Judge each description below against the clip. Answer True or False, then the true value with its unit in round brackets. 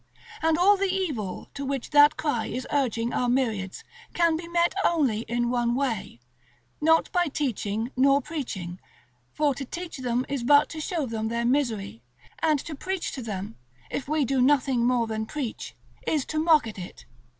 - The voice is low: False (265 Hz)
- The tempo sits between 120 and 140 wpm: False (180 wpm)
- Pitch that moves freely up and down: False (4.8 semitones)